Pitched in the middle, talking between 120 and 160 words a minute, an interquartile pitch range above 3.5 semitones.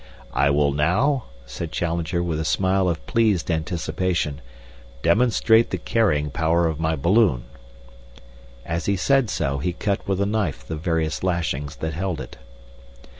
No: very low, 85 Hz; average, 150 wpm; average, 3.9 semitones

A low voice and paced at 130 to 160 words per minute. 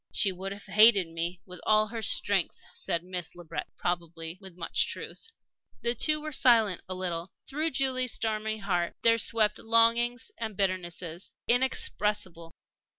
No: high, 205 Hz; average, 150 wpm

